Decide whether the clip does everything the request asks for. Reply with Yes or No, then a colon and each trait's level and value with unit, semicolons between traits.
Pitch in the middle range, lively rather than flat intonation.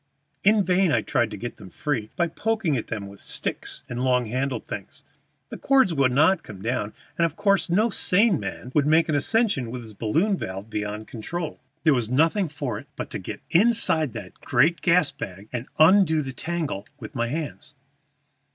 Yes: medium, 145 Hz; wide, 6.8 semitones